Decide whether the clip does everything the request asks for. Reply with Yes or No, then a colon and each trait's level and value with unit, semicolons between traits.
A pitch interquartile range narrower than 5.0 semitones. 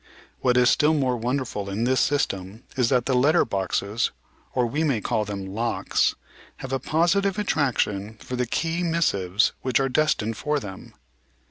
No: wide, 5.5 semitones